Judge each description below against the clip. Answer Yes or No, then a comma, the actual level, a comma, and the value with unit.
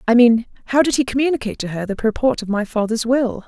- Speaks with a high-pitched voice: Yes, high, 235 Hz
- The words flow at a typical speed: No, fast, 240 wpm